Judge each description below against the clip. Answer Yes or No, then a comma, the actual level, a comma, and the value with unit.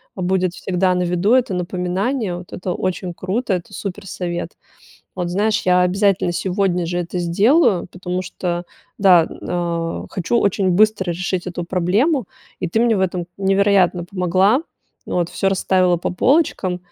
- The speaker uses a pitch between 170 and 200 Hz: Yes, medium, 185 Hz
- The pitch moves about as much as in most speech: No, narrow, 2.0 semitones